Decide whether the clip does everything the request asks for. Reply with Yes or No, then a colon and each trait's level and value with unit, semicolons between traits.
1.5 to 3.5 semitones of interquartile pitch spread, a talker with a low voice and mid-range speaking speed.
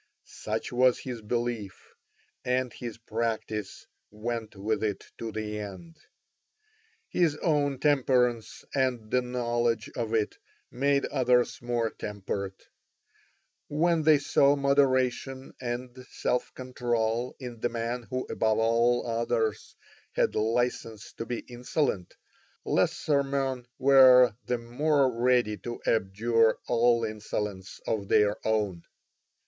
No: narrow, 2.6 semitones; low, 120 Hz; slow, 115 wpm